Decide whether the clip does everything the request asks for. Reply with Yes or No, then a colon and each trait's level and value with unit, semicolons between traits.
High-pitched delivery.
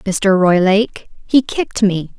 Yes: high, 200 Hz